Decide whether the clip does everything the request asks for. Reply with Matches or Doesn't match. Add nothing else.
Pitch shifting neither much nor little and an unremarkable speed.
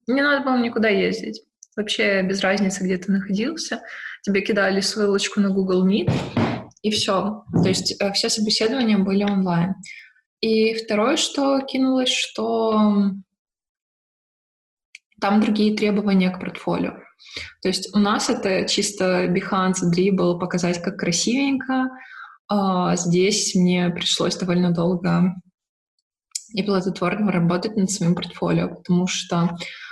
Matches